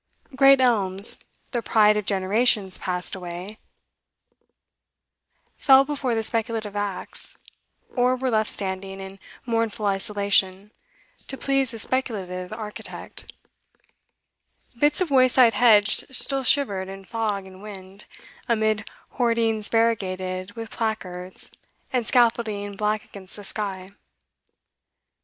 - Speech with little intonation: No, average, 3.4 semitones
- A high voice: Yes, high, 215 Hz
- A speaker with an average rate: No, slow, 110 wpm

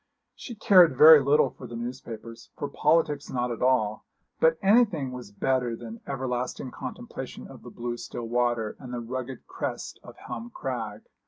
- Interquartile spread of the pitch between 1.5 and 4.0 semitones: Yes, average, 3.0 semitones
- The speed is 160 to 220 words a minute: Yes, average, 165 wpm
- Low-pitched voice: Yes, low, 125 Hz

